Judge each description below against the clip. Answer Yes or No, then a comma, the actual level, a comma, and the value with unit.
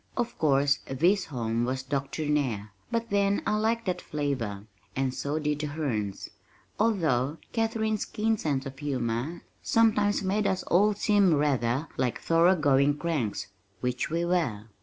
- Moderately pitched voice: Yes, medium, 150 Hz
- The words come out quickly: No, average, 145 wpm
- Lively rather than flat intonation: Yes, wide, 7.3 semitones